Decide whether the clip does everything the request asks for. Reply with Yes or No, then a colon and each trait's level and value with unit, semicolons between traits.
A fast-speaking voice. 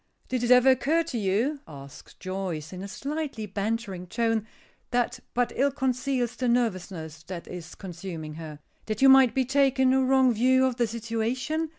No: average, 175 wpm